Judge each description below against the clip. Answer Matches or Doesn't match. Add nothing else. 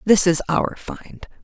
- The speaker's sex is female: Matches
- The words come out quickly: Doesn't match